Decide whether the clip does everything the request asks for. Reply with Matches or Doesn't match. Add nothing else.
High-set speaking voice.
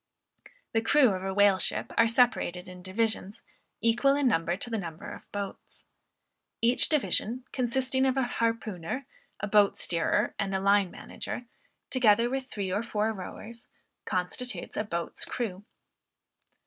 Matches